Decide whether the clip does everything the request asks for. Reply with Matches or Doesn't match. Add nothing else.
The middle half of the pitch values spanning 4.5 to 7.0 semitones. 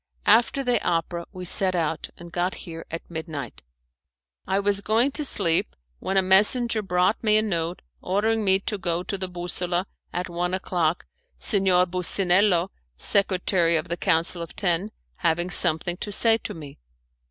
Doesn't match